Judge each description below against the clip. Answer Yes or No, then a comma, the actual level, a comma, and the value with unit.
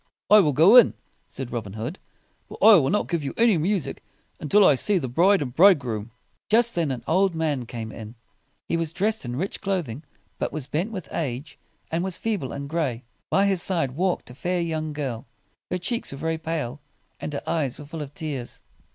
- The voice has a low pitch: No, medium, 160 Hz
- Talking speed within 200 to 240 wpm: Yes, fast, 205 wpm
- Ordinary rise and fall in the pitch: No, wide, 5.7 semitones